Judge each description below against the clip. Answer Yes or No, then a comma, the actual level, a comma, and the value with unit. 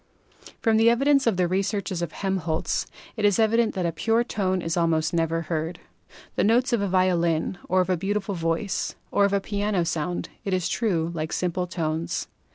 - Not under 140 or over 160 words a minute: No, average, 190 wpm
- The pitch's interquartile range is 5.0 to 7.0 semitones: No, average, 3.7 semitones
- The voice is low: No, medium, 185 Hz